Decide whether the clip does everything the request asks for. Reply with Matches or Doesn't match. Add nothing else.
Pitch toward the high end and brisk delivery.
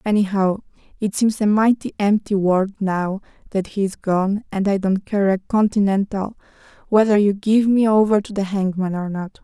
Doesn't match